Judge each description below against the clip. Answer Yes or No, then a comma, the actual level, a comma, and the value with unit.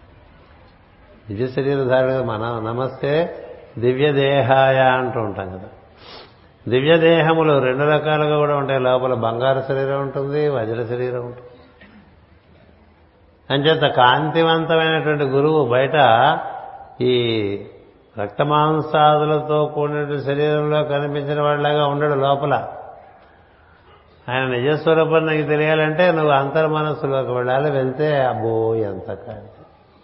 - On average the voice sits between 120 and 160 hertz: Yes, low, 135 Hz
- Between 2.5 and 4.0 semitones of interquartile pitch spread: Yes, average, 3.7 semitones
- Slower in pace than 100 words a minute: Yes, average, 90 wpm